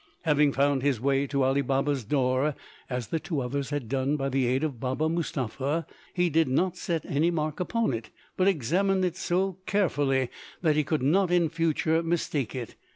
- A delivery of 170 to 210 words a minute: Yes, average, 190 wpm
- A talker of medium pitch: Yes, medium, 145 Hz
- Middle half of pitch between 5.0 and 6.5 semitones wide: No, average, 3.8 semitones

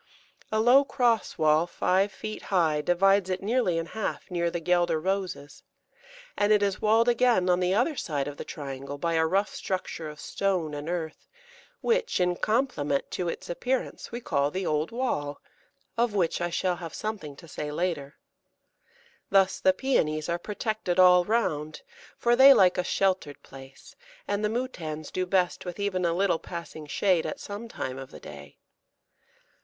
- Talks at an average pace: Yes, average, 175 wpm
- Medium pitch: Yes, medium, 180 Hz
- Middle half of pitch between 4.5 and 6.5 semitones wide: Yes, average, 4.8 semitones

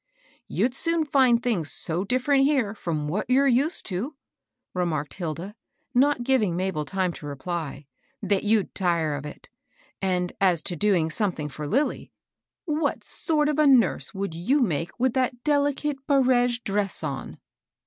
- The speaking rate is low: No, average, 160 wpm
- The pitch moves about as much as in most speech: No, wide, 7.6 semitones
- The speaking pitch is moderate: No, high, 210 Hz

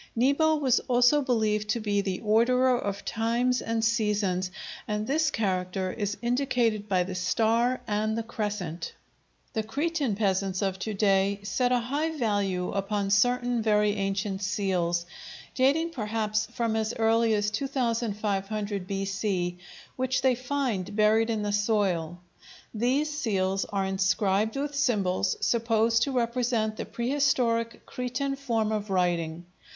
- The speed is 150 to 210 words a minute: No, slow, 135 wpm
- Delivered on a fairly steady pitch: No, average, 3.7 semitones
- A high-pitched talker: Yes, high, 215 Hz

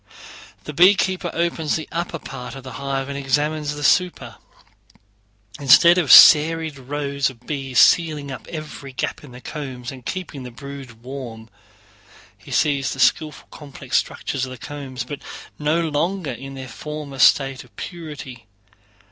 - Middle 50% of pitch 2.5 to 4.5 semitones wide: Yes, average, 2.9 semitones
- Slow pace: No, average, 155 wpm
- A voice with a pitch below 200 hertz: Yes, medium, 140 Hz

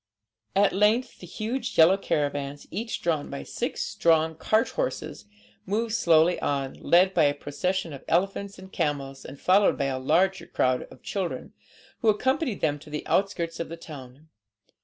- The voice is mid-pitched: Yes, medium, 170 Hz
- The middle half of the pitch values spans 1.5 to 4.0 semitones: No, wide, 5.4 semitones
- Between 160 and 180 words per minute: Yes, average, 165 wpm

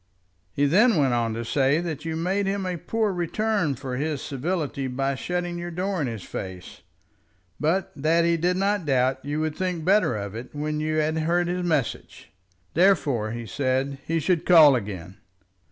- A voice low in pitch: No, medium, 155 Hz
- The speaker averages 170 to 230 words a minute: Yes, average, 185 wpm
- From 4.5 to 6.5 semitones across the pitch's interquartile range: Yes, average, 5.0 semitones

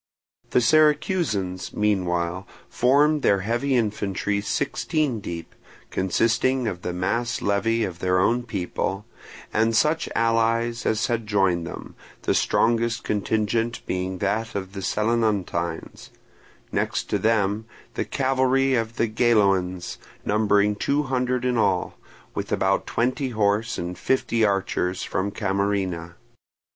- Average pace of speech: No, slow, 125 wpm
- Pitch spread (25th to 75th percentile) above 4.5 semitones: No, average, 3.6 semitones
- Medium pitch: No, low, 110 Hz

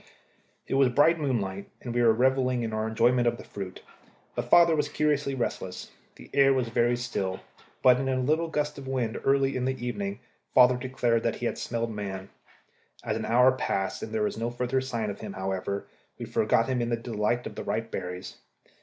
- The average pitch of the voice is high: No, low, 120 Hz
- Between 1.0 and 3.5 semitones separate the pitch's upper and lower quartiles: Yes, average, 3.2 semitones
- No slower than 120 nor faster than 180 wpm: No, fast, 205 wpm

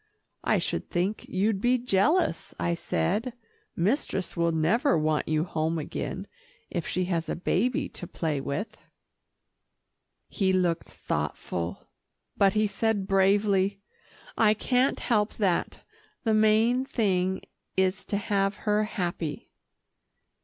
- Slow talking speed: Yes, slow, 125 wpm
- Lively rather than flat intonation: No, average, 4.0 semitones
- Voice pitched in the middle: No, high, 195 Hz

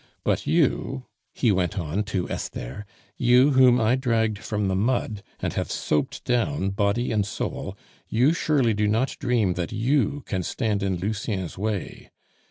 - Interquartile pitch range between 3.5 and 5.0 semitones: Yes, average, 3.9 semitones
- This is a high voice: No, low, 110 Hz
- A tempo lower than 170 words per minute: Yes, average, 160 wpm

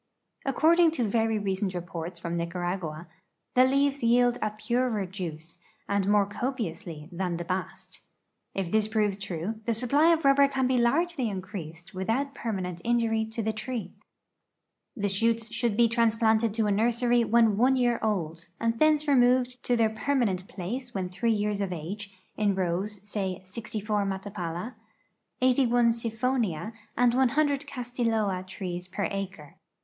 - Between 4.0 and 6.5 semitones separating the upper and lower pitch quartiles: Yes, average, 4.3 semitones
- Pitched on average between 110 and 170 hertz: No, high, 220 Hz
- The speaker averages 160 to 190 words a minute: No, average, 150 wpm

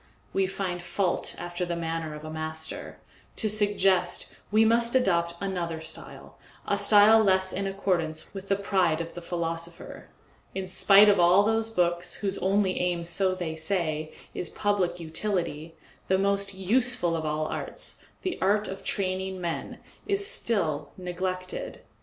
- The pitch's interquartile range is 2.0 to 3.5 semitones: Yes, average, 2.8 semitones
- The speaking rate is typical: Yes, average, 155 wpm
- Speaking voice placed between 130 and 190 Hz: Yes, medium, 185 Hz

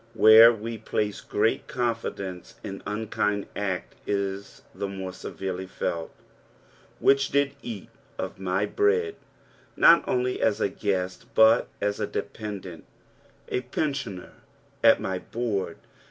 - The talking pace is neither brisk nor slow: No, slow, 125 wpm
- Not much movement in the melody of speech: No, average, 3.4 semitones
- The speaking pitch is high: No, low, 105 Hz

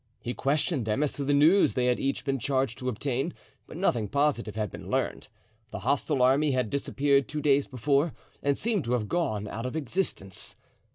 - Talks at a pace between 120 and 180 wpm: No, average, 195 wpm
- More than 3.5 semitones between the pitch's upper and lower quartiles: No, average, 3.1 semitones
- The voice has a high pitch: No, low, 135 Hz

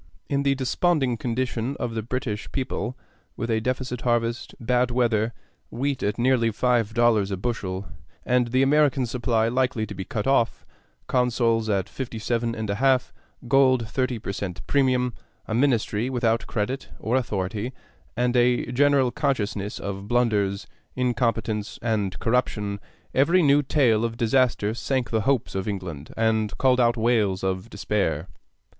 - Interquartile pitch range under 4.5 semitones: Yes, average, 3.0 semitones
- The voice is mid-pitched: No, low, 120 Hz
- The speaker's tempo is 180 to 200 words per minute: No, average, 150 wpm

